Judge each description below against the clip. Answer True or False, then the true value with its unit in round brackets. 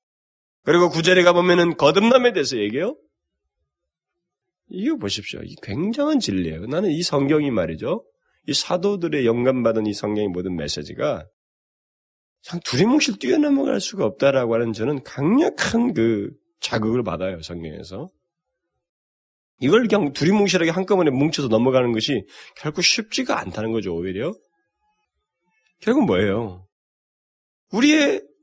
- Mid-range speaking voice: True (150 Hz)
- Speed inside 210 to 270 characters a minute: False (295 characters per minute)